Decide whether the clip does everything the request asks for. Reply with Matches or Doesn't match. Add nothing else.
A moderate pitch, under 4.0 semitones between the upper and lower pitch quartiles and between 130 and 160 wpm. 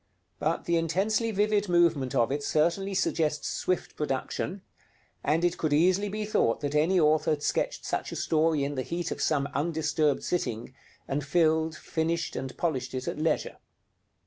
Doesn't match